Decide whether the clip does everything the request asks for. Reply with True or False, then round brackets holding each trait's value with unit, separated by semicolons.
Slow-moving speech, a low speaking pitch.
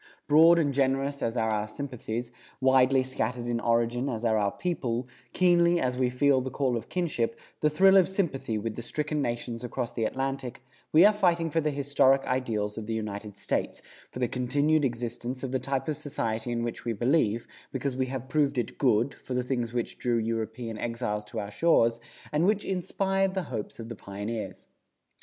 False (195 wpm; 125 Hz)